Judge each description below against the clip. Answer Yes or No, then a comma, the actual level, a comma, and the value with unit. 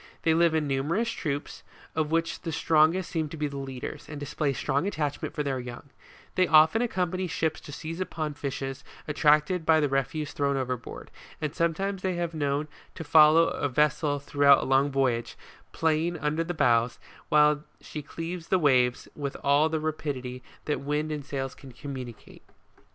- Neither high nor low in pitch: Yes, medium, 150 Hz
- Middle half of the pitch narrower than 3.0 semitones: Yes, narrow, 2.6 semitones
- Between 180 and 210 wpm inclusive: Yes, average, 185 wpm